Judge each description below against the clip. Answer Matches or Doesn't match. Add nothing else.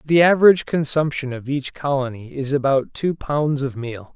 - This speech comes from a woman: Doesn't match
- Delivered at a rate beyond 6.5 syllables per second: Doesn't match